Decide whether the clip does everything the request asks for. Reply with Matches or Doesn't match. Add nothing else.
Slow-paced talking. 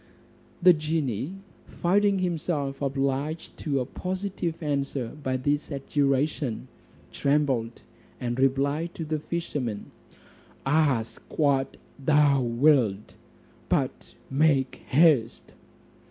Matches